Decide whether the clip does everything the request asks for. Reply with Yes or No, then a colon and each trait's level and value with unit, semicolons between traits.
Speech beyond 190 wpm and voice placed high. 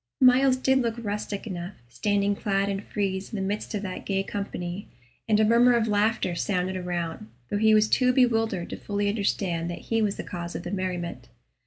Yes: average, 200 wpm; high, 200 Hz